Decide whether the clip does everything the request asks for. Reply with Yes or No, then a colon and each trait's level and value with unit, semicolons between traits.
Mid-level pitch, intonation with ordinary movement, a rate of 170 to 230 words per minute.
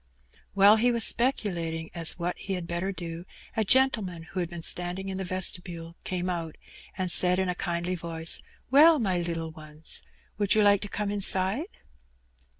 Yes: medium, 180 Hz; average, 3.0 semitones; average, 185 wpm